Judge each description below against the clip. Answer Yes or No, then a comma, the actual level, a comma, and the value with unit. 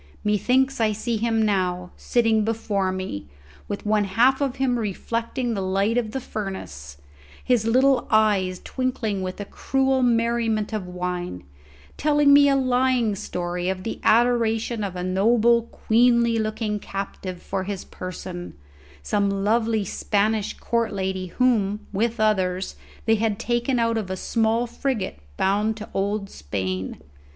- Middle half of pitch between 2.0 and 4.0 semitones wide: Yes, average, 3.7 semitones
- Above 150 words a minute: No, average, 145 wpm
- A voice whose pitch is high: Yes, high, 215 Hz